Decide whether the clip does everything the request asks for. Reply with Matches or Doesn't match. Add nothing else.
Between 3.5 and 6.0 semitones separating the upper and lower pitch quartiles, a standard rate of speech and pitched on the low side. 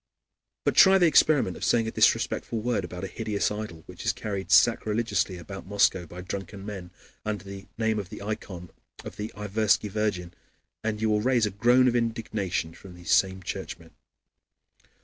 Doesn't match